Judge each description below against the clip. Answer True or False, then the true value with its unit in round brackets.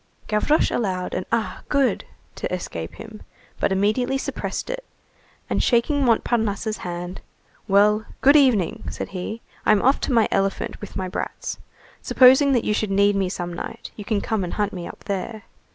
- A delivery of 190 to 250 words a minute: False (175 wpm)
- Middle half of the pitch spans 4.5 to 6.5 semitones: False (3.8 semitones)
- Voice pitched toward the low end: False (210 Hz)